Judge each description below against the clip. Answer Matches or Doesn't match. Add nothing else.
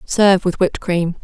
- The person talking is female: Matches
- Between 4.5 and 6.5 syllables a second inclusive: Matches